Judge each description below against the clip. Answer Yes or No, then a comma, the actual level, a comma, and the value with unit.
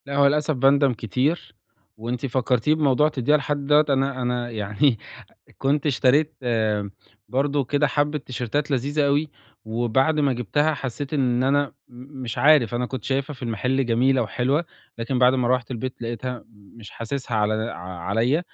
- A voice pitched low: Yes, low, 130 Hz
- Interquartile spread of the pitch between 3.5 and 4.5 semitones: No, average, 3.1 semitones